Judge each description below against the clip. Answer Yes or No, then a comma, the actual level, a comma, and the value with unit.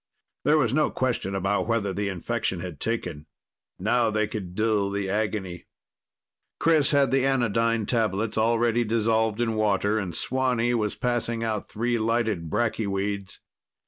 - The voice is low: Yes, low, 110 Hz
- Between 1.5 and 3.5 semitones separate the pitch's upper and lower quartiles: Yes, average, 2.9 semitones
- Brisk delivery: No, average, 145 wpm